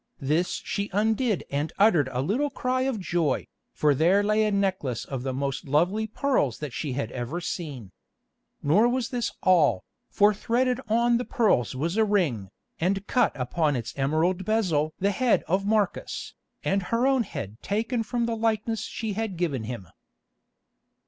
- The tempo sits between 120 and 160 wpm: No, average, 170 wpm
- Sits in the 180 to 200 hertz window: Yes, high, 190 Hz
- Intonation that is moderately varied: No, wide, 7.4 semitones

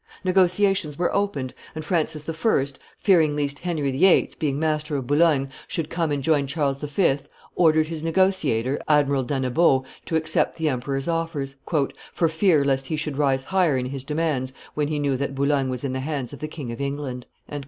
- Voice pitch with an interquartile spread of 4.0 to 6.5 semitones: No, average, 3.1 semitones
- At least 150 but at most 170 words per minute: No, average, 185 wpm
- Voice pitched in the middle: Yes, medium, 150 Hz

